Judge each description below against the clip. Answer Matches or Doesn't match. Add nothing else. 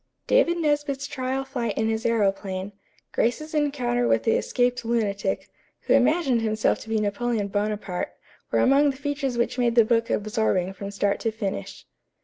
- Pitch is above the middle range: Matches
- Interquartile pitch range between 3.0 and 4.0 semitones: Doesn't match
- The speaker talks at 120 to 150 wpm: Doesn't match